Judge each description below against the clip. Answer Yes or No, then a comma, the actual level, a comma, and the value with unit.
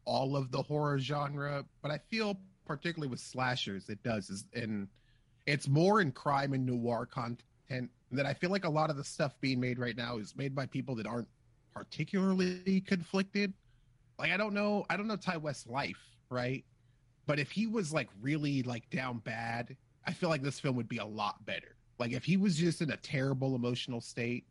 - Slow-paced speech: No, fast, 205 wpm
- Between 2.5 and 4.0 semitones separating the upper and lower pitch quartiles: No, average, 4.4 semitones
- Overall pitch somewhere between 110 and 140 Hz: Yes, low, 135 Hz